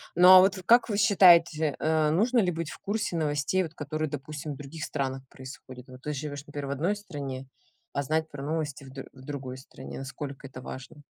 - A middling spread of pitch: Yes, average, 3.7 semitones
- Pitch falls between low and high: Yes, medium, 150 Hz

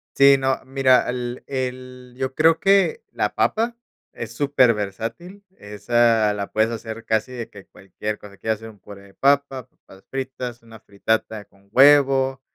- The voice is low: Yes, low, 125 Hz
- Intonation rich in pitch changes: No, average, 3.7 semitones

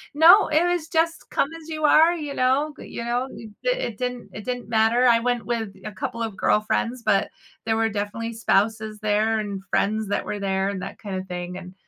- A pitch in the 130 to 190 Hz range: No, high, 225 Hz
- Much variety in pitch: No, average, 3.7 semitones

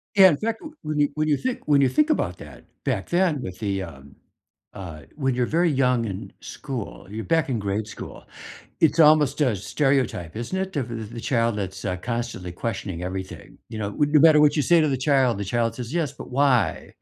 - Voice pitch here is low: Yes, low, 125 Hz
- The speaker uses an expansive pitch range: Yes, wide, 6.3 semitones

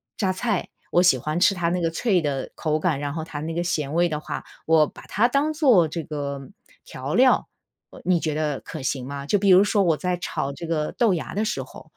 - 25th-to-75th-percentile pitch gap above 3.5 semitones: Yes, average, 3.9 semitones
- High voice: No, medium, 165 Hz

